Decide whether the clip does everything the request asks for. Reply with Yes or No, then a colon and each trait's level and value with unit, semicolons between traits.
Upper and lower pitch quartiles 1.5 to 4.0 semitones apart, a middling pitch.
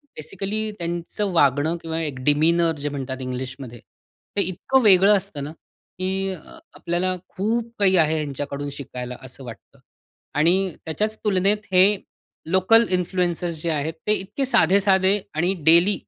No: average, 4.7 semitones; medium, 175 Hz